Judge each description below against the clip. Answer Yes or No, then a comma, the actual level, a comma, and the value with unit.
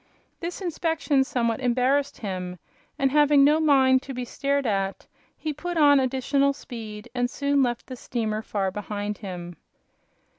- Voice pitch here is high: Yes, very high, 260 Hz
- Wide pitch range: No, average, 4.8 semitones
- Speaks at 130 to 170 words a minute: Yes, average, 150 wpm